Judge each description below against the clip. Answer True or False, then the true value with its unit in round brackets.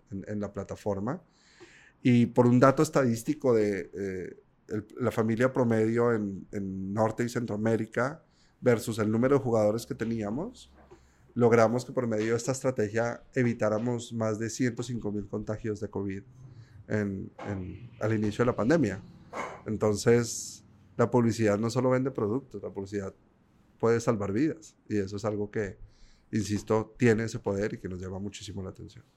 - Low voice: True (110 Hz)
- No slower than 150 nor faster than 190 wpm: True (160 wpm)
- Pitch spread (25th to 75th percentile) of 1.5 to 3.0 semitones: True (2.5 semitones)